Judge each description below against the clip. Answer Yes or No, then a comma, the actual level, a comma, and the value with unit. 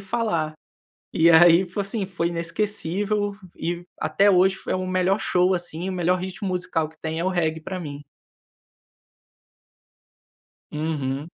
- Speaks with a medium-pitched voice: Yes, medium, 175 Hz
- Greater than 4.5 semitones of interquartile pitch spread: No, average, 2.8 semitones